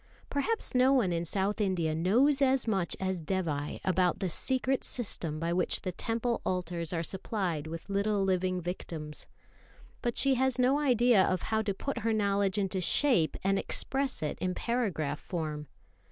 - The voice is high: Yes, high, 195 Hz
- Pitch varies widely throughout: Yes, wide, 5.7 semitones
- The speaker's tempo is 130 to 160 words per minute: No, average, 170 wpm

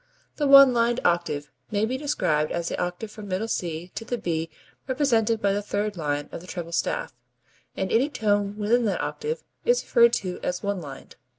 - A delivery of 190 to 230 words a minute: Yes, average, 195 wpm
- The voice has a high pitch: Yes, high, 205 Hz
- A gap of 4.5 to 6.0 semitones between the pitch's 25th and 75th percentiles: Yes, average, 5.2 semitones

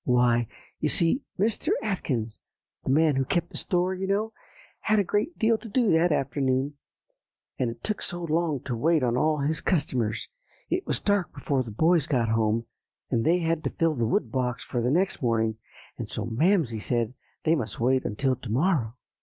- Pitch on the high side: No, medium, 140 Hz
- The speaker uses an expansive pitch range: Yes, wide, 6.7 semitones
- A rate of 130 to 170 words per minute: No, average, 195 wpm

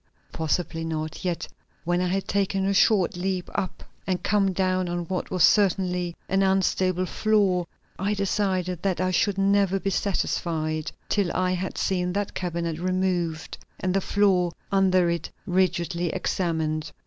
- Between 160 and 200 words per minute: No, average, 150 wpm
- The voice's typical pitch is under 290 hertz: Yes, medium, 185 Hz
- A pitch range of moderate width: No, narrow, 1.8 semitones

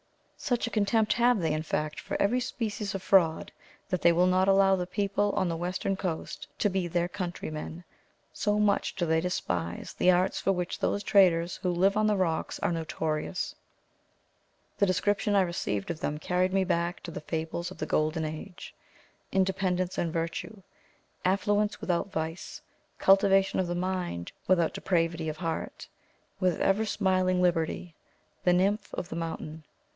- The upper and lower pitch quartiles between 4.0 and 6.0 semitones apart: No, average, 2.8 semitones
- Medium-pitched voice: Yes, medium, 180 Hz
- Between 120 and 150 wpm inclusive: No, average, 165 wpm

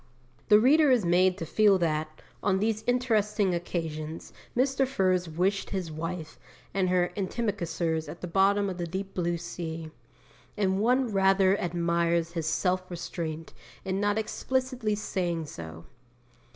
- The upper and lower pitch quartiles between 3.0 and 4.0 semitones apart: Yes, average, 3.4 semitones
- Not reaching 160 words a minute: Yes, average, 140 wpm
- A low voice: No, medium, 185 Hz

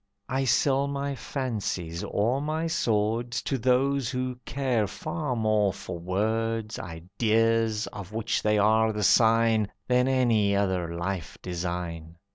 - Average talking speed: No, slow, 130 wpm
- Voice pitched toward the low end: Yes, low, 110 Hz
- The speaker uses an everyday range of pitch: Yes, average, 4.1 semitones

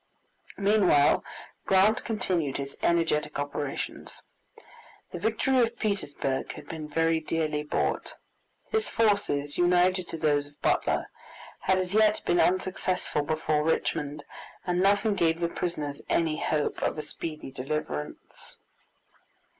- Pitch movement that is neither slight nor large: Yes, average, 4.1 semitones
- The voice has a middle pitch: Yes, medium, 165 Hz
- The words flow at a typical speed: No, slow, 120 wpm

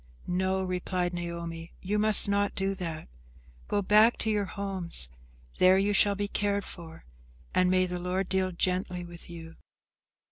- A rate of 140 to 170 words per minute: Yes, average, 155 wpm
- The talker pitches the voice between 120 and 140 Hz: No, medium, 185 Hz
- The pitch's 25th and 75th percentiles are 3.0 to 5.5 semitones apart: No, narrow, 2.4 semitones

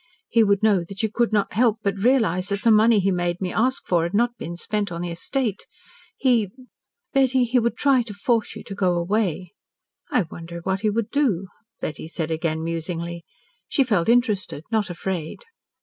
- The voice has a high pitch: Yes, high, 200 Hz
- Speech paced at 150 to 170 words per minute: No, average, 195 wpm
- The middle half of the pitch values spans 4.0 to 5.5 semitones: Yes, average, 5.0 semitones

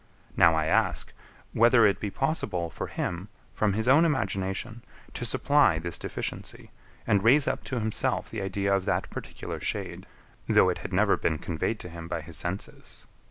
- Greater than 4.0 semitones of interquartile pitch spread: Yes, average, 5.3 semitones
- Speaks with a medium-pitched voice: No, low, 100 Hz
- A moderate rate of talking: Yes, average, 175 wpm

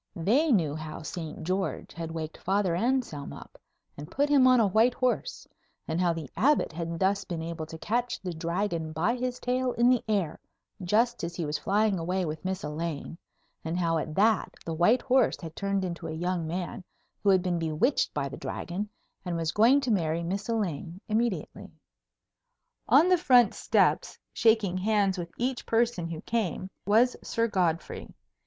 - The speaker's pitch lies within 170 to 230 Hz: Yes, medium, 185 Hz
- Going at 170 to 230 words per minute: Yes, average, 180 wpm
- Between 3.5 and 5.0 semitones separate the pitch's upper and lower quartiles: No, wide, 5.6 semitones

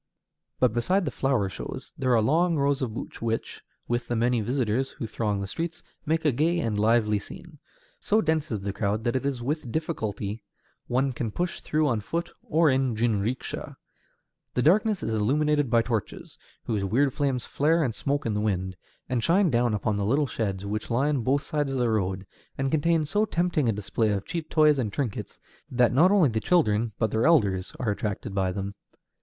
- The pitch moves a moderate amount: No, wide, 5.8 semitones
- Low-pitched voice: Yes, low, 125 Hz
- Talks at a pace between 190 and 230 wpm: Yes, average, 200 wpm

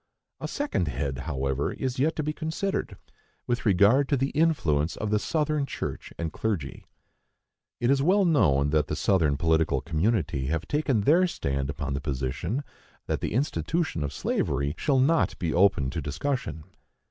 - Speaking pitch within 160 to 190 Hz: No, low, 100 Hz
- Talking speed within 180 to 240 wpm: No, average, 165 wpm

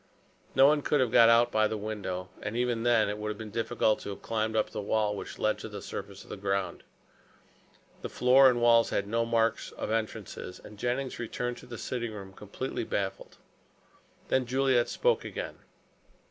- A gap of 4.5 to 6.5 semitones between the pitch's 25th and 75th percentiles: No, narrow, 2.5 semitones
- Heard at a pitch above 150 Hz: No, low, 115 Hz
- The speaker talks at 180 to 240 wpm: Yes, average, 195 wpm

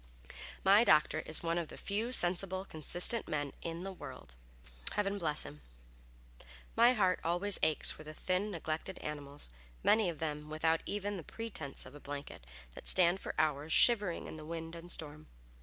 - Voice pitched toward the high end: No, medium, 170 Hz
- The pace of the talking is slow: No, average, 175 wpm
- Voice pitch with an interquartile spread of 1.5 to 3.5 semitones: No, average, 4.2 semitones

